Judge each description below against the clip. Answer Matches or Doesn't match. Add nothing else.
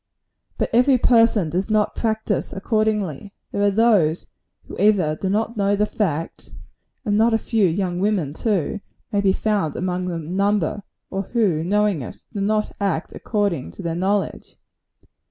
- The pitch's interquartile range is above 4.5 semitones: Doesn't match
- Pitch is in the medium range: Doesn't match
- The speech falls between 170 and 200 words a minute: Doesn't match